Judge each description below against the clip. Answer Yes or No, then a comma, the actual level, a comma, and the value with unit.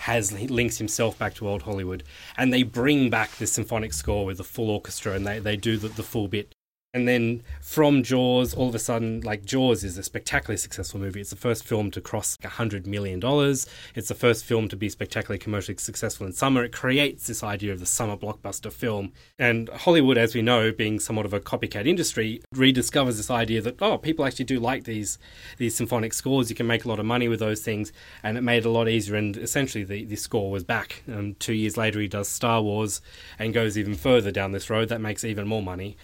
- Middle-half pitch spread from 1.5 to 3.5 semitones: Yes, average, 2.7 semitones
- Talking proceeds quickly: Yes, fast, 230 wpm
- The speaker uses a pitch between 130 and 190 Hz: No, low, 110 Hz